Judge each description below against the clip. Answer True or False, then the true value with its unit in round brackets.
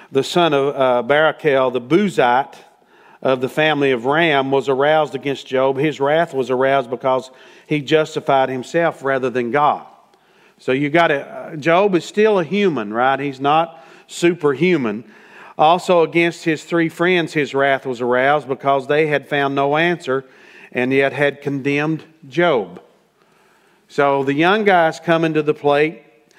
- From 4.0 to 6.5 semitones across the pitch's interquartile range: False (3.2 semitones)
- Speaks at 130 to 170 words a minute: True (150 wpm)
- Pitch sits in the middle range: True (145 Hz)